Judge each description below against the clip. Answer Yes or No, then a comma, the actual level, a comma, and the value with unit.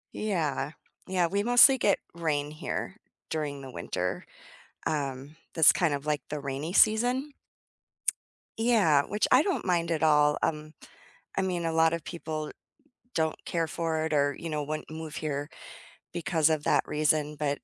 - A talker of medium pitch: Yes, medium, 155 Hz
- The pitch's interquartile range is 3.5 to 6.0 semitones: No, average, 2.7 semitones